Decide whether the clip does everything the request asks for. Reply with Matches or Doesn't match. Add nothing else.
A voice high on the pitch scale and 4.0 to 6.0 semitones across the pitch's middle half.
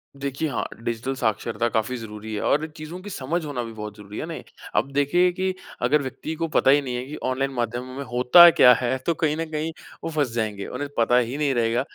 Doesn't match